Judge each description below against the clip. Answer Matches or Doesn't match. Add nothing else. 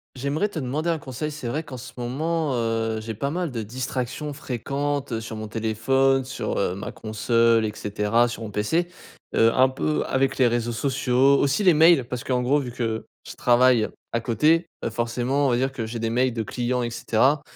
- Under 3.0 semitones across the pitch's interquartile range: Doesn't match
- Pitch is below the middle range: Matches